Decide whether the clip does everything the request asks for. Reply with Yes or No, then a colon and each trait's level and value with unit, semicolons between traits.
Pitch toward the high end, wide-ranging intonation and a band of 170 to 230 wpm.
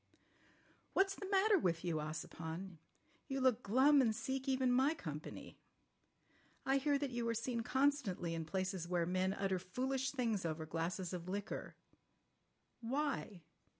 No: high, 220 Hz; wide, 7.1 semitones; average, 145 wpm